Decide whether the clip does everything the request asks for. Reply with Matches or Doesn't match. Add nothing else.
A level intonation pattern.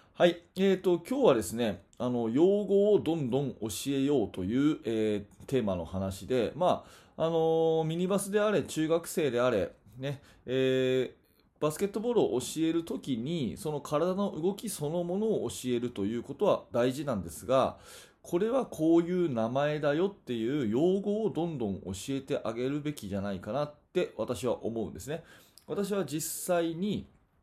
Doesn't match